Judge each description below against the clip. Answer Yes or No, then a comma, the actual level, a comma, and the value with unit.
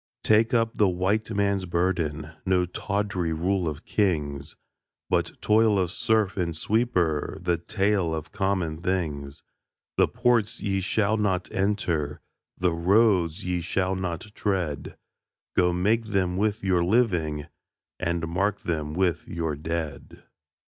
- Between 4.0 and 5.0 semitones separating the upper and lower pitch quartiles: No, average, 3.6 semitones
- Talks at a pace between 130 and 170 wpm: Yes, slow, 135 wpm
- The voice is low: Yes, very low, 90 Hz